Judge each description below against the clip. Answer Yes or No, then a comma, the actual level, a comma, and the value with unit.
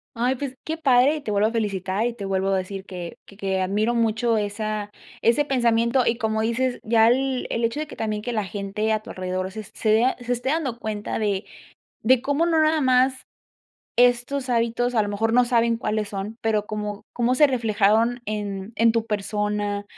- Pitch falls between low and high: No, high, 225 Hz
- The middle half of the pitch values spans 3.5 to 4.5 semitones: No, average, 3.0 semitones